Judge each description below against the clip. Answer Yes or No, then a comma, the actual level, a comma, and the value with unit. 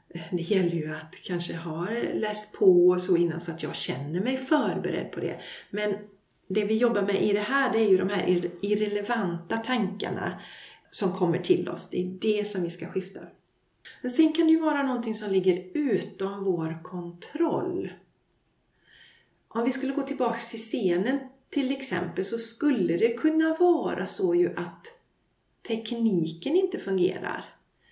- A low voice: No, high, 205 Hz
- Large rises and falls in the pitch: Yes, wide, 6.5 semitones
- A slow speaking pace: No, average, 165 wpm